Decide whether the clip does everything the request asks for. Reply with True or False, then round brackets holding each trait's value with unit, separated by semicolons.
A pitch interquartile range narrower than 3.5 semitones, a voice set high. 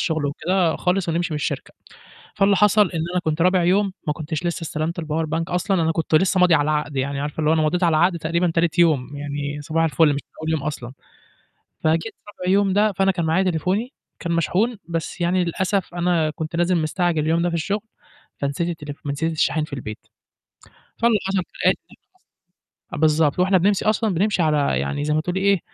False (3.0 semitones; 170 Hz)